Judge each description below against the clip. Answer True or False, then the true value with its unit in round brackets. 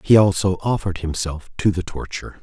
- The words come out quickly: False (175 wpm)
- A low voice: True (90 Hz)